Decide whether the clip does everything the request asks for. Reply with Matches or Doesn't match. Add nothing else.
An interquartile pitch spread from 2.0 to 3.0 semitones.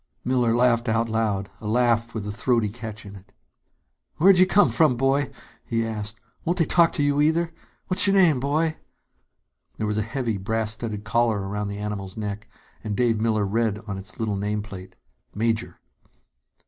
Doesn't match